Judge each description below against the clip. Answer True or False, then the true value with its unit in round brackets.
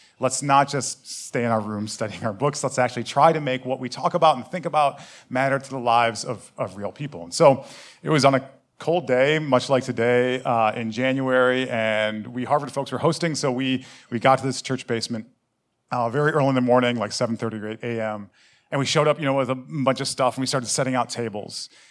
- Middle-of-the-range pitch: False (130 Hz)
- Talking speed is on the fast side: True (235 wpm)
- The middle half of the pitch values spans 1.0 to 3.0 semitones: True (2.5 semitones)